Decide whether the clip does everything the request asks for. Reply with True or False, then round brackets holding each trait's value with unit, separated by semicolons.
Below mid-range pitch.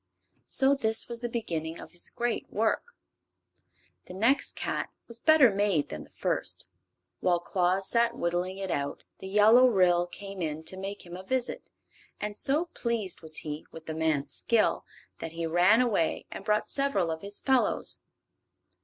False (195 Hz)